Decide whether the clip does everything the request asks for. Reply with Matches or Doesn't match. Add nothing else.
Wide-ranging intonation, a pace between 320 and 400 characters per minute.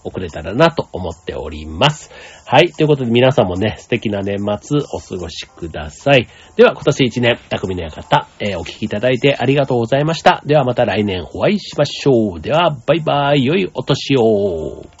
Matches